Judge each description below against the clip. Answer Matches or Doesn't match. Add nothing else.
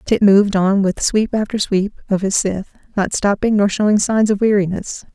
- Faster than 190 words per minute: Matches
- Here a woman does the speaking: Matches